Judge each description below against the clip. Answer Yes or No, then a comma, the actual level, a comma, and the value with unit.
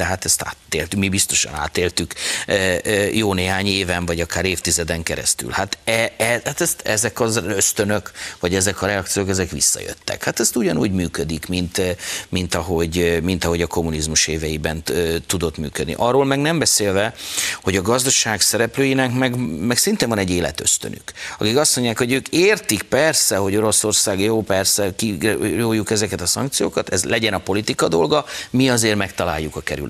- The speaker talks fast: Yes, fast, 170 wpm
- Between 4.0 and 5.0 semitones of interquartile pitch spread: Yes, average, 4.7 semitones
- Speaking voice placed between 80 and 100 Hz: Yes, very low, 95 Hz